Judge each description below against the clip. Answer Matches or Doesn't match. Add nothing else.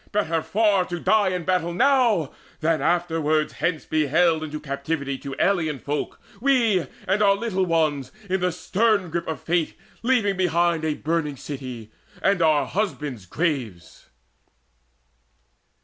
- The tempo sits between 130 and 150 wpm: Matches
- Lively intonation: Doesn't match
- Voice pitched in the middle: Matches